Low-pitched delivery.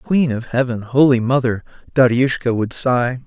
Yes: low, 125 Hz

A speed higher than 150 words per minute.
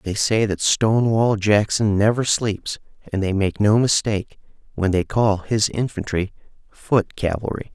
No: average, 145 wpm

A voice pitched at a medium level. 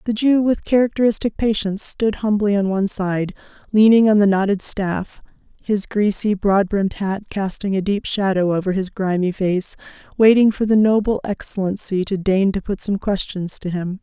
No: high, 200 Hz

